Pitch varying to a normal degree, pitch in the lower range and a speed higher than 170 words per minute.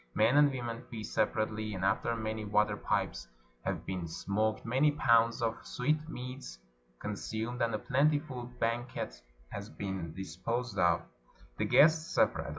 No: average, 3.4 semitones; low, 115 Hz; average, 145 wpm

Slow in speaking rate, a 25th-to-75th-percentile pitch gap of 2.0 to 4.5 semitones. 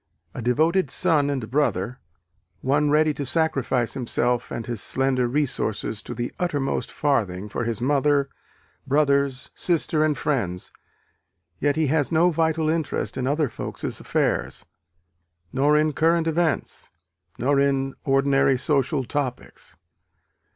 Yes: slow, 130 wpm; average, 3.4 semitones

